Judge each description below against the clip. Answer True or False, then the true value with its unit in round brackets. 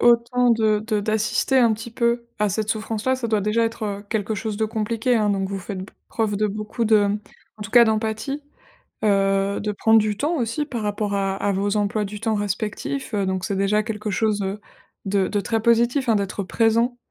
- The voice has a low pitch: False (215 Hz)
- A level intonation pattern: True (2.1 semitones)